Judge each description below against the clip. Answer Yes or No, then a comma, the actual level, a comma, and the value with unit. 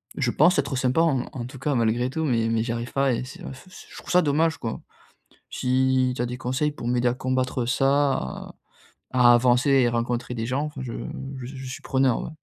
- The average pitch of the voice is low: Yes, low, 130 Hz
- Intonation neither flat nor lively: No, narrow, 2.1 semitones